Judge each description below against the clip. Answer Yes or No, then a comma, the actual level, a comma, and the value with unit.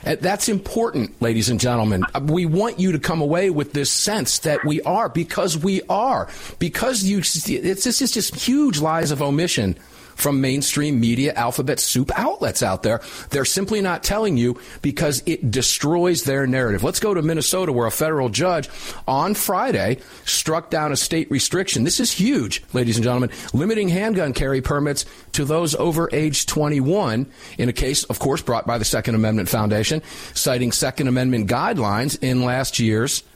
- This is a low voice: No, medium, 145 Hz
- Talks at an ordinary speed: Yes, average, 175 wpm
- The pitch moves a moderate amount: No, wide, 6.0 semitones